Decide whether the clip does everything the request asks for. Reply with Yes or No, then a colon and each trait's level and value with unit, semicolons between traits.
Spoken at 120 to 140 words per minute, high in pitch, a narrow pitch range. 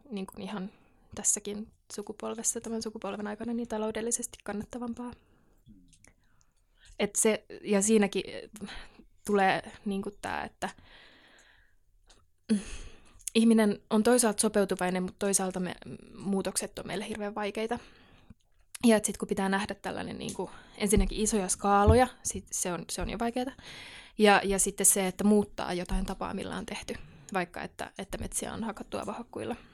Yes: average, 135 wpm; high, 205 Hz; narrow, 2.2 semitones